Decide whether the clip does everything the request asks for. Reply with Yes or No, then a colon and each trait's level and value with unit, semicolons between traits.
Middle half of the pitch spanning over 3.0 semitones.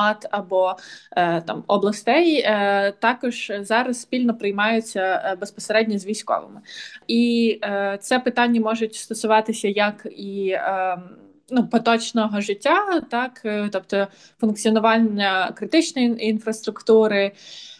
No: average, 2.7 semitones